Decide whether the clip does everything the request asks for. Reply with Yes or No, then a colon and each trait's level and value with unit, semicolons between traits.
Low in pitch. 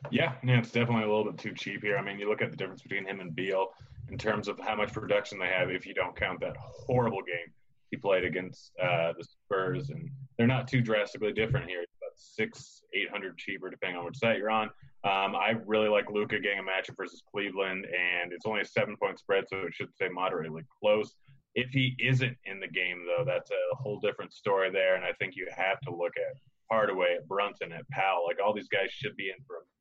Yes: low, 110 Hz